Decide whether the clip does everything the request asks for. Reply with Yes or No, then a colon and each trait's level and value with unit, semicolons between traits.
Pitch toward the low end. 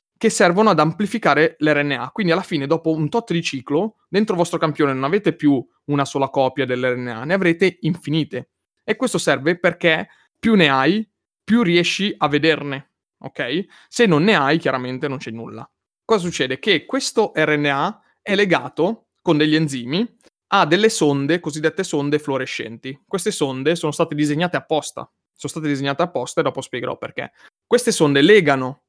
No: medium, 155 Hz